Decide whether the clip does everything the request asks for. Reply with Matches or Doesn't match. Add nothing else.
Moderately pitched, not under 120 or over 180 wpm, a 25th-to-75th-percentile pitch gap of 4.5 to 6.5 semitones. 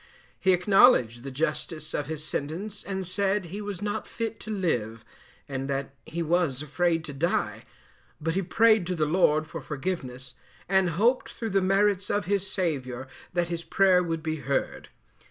Matches